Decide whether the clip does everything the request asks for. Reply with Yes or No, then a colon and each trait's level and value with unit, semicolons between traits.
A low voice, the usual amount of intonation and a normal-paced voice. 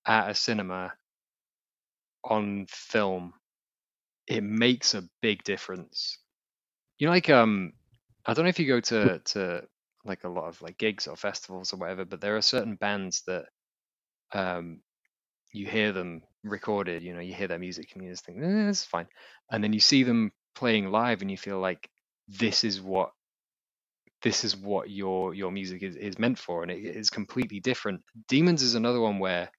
Yes: low, 105 Hz; average, 3.7 semitones; average, 185 wpm